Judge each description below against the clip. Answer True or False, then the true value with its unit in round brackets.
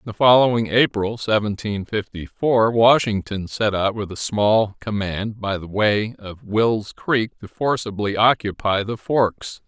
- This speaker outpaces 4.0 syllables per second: False (3.7 syllables/s)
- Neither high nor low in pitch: False (105 Hz)